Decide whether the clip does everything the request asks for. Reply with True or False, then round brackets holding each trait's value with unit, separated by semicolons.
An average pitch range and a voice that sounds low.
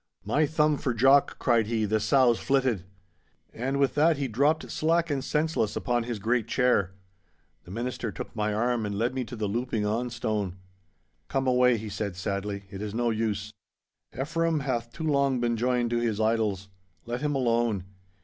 True (3.8 semitones; 120 Hz)